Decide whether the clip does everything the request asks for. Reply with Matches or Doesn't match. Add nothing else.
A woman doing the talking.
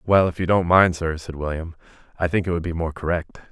Doesn't match